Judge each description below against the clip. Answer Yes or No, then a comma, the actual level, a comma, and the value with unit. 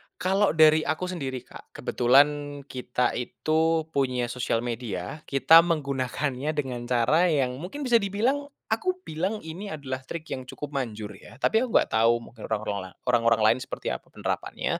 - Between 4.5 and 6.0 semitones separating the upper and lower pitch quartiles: Yes, average, 5.0 semitones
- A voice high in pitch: No, medium, 140 Hz